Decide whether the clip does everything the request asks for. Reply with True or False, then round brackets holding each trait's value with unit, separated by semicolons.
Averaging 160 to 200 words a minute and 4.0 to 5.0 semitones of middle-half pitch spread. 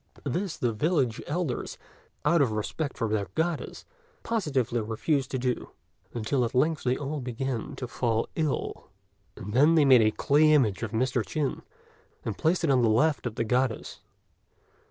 True (170 wpm; 4.7 semitones)